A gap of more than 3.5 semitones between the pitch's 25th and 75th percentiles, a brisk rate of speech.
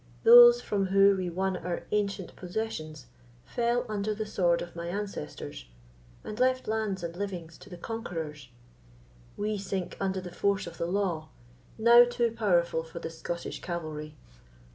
No: average, 3.9 semitones; average, 155 wpm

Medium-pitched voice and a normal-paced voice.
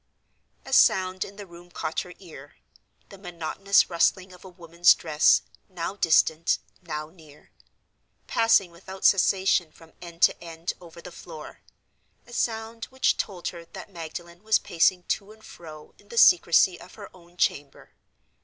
Yes: medium, 175 Hz; average, 150 wpm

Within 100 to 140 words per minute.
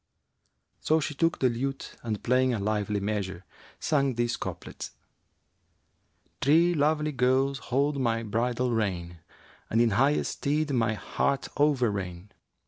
Yes: slow, 135 wpm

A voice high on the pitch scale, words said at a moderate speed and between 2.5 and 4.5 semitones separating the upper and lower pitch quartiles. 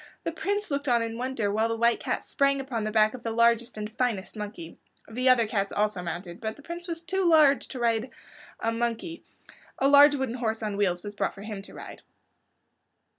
No: high, 230 Hz; fast, 220 wpm; average, 4.1 semitones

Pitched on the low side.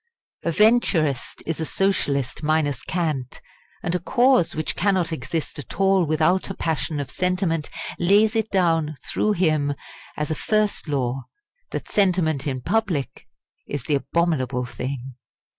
No: medium, 160 Hz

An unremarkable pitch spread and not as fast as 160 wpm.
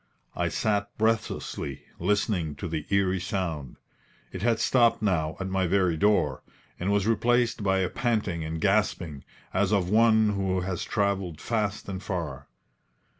Yes: average, 3.3 semitones; average, 150 wpm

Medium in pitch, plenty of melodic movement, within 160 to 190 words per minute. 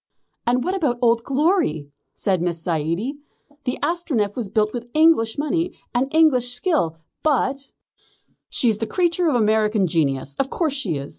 No: high, 245 Hz; wide, 7.0 semitones; average, 165 wpm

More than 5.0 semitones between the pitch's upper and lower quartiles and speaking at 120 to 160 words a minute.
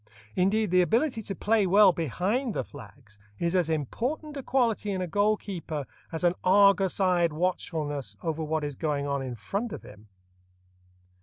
No: wide, 5.4 semitones; average, 170 wpm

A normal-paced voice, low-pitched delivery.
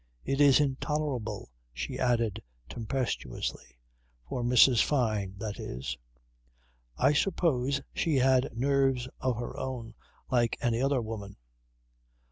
No: slow, 110 wpm; low, 125 Hz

